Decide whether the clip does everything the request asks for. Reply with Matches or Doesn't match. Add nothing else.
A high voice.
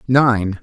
Doesn't match